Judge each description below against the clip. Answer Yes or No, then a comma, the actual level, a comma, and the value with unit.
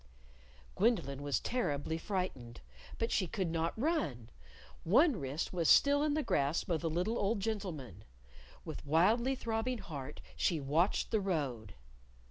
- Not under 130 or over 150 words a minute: Yes, average, 145 wpm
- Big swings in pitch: Yes, wide, 7.7 semitones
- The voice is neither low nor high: Yes, medium, 175 Hz